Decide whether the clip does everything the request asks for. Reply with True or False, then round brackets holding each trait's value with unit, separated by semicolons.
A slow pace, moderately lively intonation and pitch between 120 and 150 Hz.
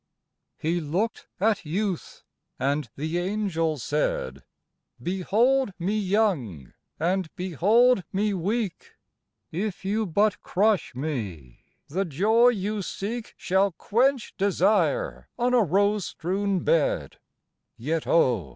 False (110 wpm; 5.0 semitones; 190 Hz)